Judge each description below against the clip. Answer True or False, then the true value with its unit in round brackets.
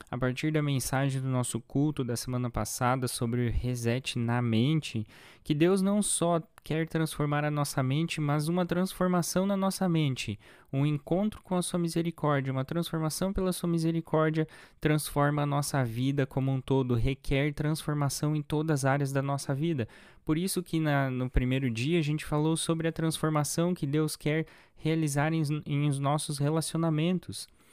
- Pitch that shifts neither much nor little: True (3.4 semitones)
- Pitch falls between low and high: True (150 Hz)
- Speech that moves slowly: False (170 wpm)